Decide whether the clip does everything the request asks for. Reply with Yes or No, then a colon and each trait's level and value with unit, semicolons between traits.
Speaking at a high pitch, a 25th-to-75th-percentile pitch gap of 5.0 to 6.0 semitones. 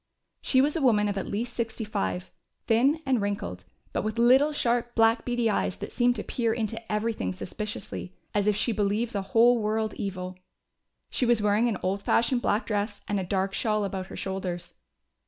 No: high, 215 Hz; average, 3.2 semitones